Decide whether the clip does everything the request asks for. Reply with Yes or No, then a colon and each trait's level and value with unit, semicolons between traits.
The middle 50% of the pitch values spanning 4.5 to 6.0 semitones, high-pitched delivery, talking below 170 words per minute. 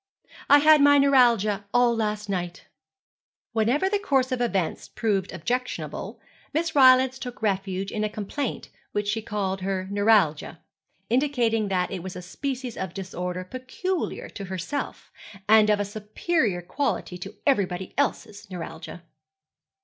Yes: average, 5.2 semitones; high, 215 Hz; average, 140 wpm